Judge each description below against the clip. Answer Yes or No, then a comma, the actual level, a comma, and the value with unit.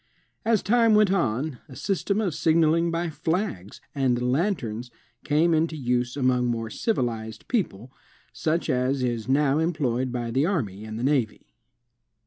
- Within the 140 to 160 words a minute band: Yes, average, 145 wpm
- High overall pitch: No, low, 135 Hz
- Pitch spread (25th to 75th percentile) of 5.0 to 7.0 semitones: Yes, wide, 5.5 semitones